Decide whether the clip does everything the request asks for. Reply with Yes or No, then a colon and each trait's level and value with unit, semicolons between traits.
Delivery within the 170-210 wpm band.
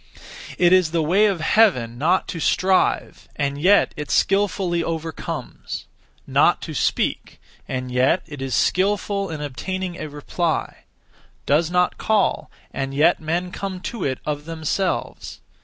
No: average, 140 wpm